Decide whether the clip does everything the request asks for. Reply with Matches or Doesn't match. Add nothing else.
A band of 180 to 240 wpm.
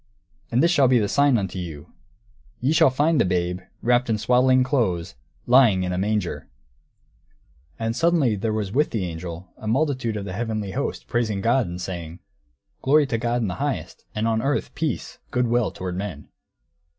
Matches